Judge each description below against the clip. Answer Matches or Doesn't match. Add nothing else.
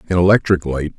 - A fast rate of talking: Doesn't match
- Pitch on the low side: Matches